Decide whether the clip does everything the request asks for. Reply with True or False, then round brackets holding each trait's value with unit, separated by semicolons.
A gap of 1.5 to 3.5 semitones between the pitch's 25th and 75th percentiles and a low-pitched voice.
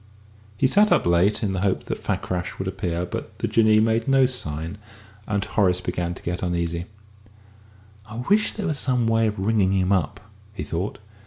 False (4.3 semitones; 100 Hz)